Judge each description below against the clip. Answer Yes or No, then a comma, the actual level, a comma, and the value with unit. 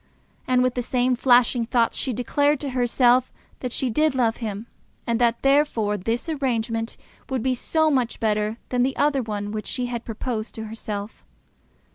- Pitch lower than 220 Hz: No, high, 245 Hz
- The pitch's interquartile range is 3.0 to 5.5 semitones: No, narrow, 2.5 semitones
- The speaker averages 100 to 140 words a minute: No, average, 175 wpm